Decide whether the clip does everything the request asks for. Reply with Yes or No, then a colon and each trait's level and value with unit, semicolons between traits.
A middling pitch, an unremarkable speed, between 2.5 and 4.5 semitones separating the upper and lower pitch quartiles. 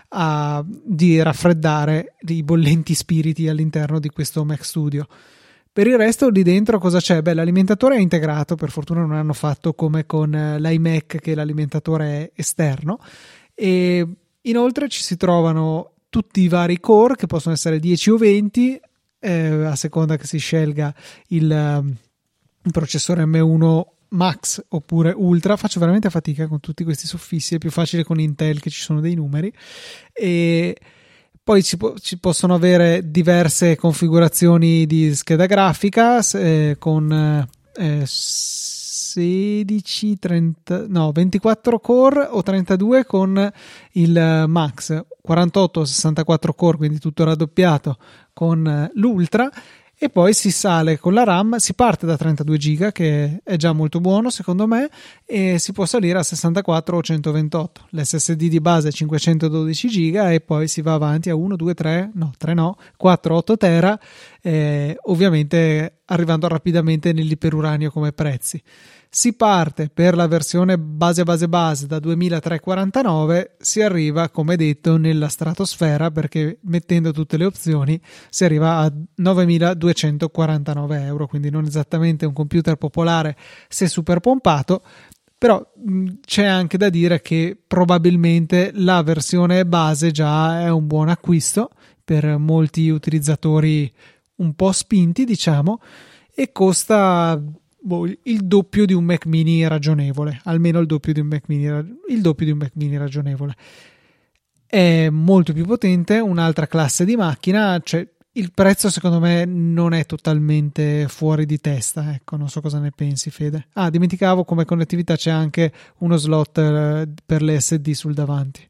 Yes: medium, 165 Hz; average, 145 wpm; average, 2.8 semitones